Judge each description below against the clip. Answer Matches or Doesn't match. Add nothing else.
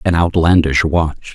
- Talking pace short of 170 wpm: Matches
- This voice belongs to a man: Matches